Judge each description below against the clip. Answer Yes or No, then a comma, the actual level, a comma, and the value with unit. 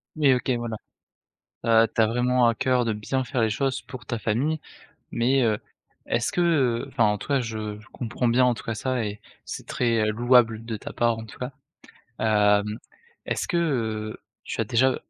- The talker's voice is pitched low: Yes, low, 115 Hz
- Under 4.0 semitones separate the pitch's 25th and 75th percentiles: Yes, average, 2.7 semitones